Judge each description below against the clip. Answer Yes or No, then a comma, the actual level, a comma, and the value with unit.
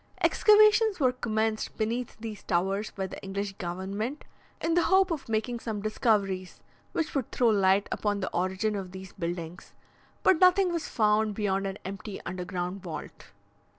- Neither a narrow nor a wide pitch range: Yes, average, 4.3 semitones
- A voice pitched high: Yes, high, 210 Hz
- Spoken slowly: No, average, 155 wpm